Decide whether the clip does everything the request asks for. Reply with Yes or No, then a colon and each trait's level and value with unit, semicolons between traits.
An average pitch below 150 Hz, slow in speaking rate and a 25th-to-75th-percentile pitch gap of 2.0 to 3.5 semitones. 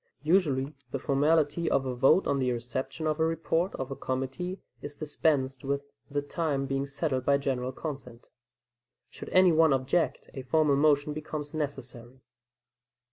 No: medium, 140 Hz; average, 155 wpm; average, 2.8 semitones